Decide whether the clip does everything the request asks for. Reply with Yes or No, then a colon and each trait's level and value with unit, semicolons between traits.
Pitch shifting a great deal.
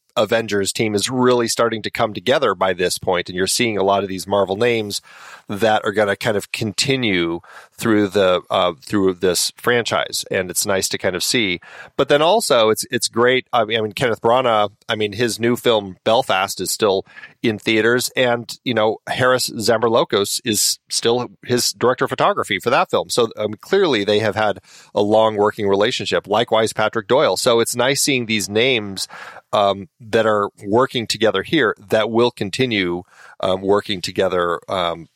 No: average, 2.8 semitones